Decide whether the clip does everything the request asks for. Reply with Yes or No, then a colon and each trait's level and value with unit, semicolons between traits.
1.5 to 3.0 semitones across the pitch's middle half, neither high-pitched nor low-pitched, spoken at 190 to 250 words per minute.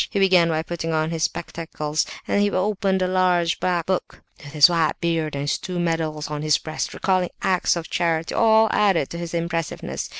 Yes: narrow, 2.5 semitones; medium, 170 Hz; average, 195 wpm